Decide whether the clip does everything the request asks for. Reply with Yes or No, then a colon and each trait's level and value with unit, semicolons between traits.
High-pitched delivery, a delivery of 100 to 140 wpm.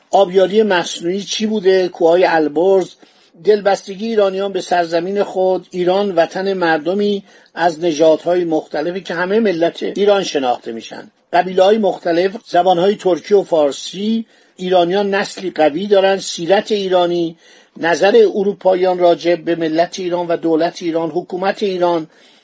No: medium, 180 Hz; average, 130 wpm